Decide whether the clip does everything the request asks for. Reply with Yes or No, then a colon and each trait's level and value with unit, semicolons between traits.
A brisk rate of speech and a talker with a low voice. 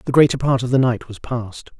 Yes: fast, 270 wpm; low, 125 Hz